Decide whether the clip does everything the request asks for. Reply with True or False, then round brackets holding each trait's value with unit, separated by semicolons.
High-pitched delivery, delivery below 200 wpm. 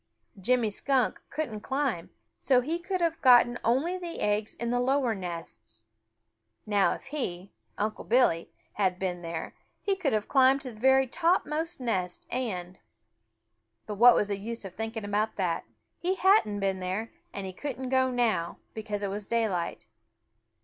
True (225 Hz; 165 wpm)